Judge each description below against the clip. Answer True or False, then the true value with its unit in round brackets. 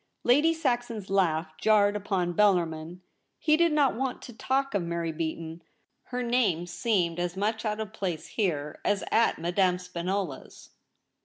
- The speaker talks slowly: False (150 wpm)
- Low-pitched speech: False (195 Hz)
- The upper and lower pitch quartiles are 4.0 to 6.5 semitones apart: True (5.2 semitones)